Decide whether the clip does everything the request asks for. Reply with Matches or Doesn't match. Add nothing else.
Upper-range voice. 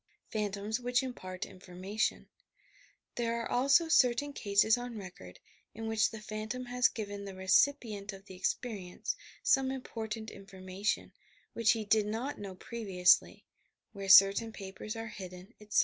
Matches